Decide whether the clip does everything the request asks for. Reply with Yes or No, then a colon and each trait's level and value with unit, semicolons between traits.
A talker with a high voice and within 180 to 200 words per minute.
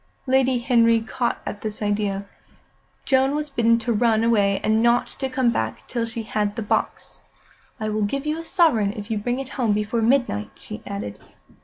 Yes: high, 230 Hz; average, 190 wpm